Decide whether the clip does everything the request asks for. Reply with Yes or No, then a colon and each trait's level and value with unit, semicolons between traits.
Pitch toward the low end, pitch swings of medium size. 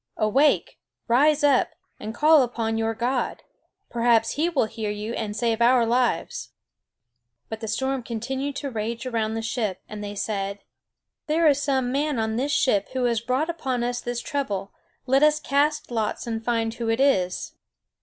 No: high, 240 Hz; average, 3.6 semitones